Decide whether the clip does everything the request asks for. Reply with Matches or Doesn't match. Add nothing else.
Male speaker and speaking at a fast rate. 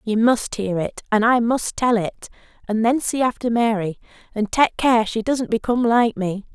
Doesn't match